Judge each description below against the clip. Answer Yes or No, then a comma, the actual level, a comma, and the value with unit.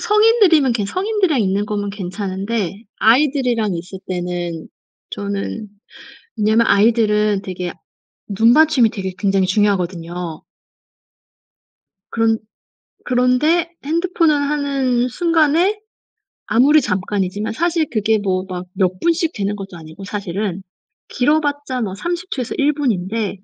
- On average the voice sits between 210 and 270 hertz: Yes, high, 220 Hz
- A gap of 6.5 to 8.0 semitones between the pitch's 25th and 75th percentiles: Yes, wide, 7.0 semitones